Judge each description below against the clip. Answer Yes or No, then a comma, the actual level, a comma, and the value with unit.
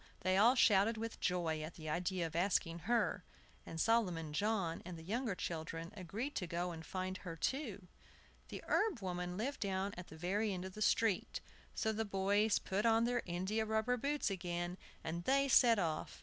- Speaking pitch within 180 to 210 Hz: Yes, high, 190 Hz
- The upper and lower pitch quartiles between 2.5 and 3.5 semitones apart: No, average, 4.3 semitones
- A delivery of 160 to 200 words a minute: Yes, average, 190 wpm